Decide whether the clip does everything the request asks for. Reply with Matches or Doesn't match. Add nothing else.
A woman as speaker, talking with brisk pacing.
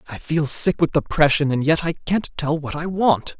Doesn't match